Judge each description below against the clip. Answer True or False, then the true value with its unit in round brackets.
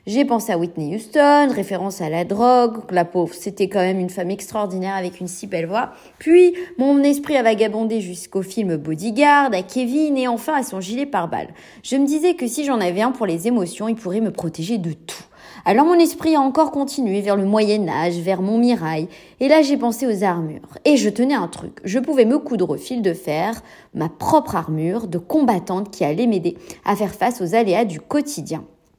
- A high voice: True (220 Hz)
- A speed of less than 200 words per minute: False (210 wpm)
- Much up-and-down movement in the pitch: True (6.4 semitones)